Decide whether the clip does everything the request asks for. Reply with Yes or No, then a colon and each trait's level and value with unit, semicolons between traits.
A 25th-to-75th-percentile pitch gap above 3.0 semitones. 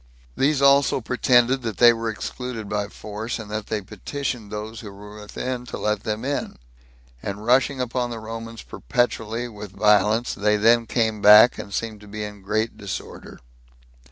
No: narrow, 2.5 semitones